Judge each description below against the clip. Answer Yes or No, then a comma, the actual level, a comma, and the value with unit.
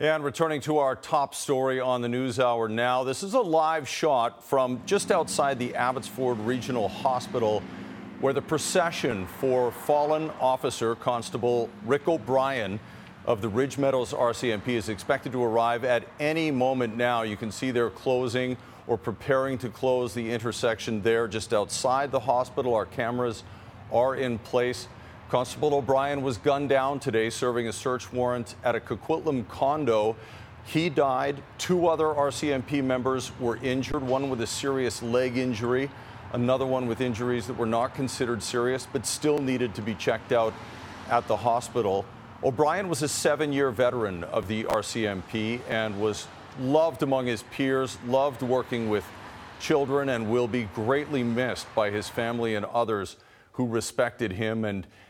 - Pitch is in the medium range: No, low, 125 Hz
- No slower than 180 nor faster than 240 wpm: No, average, 160 wpm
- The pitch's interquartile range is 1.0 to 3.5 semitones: Yes, average, 2.7 semitones